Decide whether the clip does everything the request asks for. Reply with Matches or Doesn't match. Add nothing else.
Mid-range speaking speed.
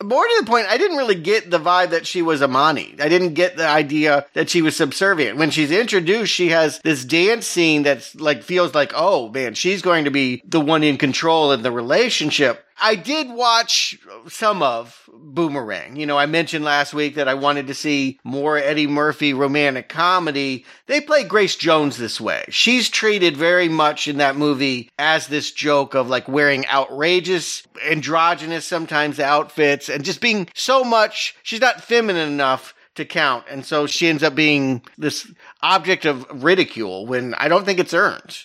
Matches